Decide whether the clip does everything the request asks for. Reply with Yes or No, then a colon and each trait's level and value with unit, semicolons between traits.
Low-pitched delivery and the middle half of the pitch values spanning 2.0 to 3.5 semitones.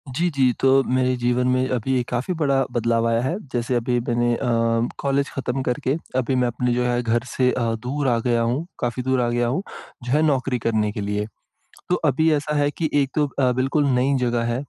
Yes: low, 125 Hz; narrow, 2.4 semitones